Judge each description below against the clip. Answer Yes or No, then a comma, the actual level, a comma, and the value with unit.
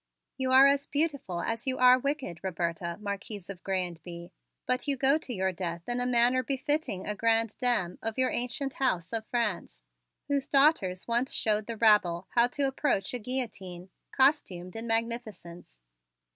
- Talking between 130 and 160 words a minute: No, average, 170 wpm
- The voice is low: No, high, 230 Hz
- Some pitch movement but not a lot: No, wide, 5.8 semitones